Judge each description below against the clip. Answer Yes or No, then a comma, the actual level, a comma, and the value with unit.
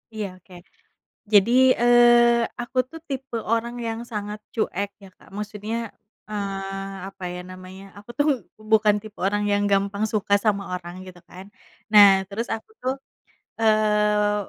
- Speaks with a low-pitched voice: No, high, 210 Hz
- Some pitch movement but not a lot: No, narrow, 2.3 semitones